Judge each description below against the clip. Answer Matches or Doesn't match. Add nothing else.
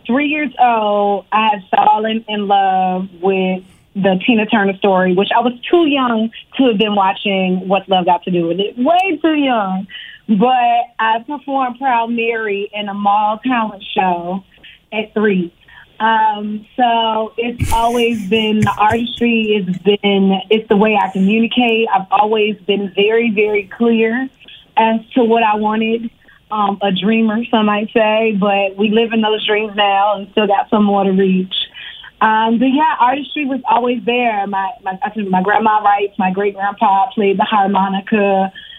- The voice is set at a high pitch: Matches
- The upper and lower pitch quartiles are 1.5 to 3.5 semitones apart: Matches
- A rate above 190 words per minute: Doesn't match